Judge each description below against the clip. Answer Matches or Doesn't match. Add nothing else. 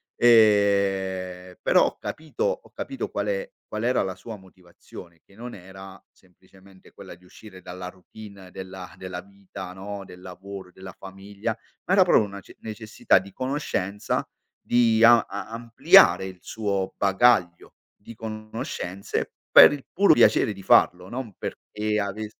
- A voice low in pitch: Matches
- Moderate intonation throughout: Matches